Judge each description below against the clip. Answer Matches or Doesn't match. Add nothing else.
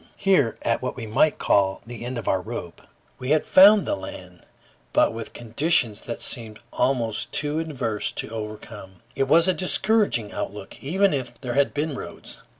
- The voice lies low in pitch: Matches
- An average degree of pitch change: Doesn't match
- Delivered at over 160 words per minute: Matches